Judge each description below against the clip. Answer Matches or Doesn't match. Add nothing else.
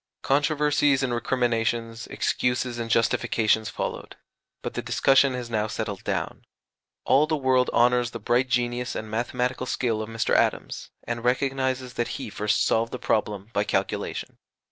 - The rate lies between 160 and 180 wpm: Doesn't match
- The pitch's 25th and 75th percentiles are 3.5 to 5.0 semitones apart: Doesn't match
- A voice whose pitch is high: Doesn't match